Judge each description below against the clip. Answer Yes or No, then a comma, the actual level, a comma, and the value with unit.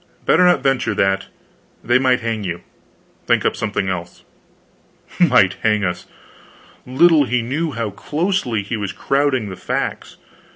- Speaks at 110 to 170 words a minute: Yes, average, 140 wpm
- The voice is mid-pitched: No, low, 120 Hz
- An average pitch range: No, wide, 5.7 semitones